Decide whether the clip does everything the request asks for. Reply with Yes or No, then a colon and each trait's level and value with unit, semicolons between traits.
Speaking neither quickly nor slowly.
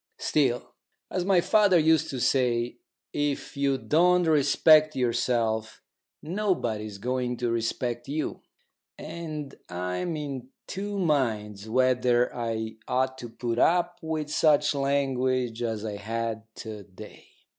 No: slow, 125 wpm